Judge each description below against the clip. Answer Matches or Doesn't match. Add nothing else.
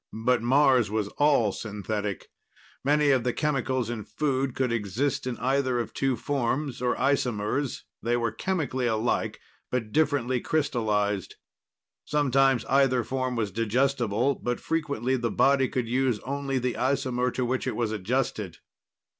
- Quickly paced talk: Doesn't match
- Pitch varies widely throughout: Doesn't match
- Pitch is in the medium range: Doesn't match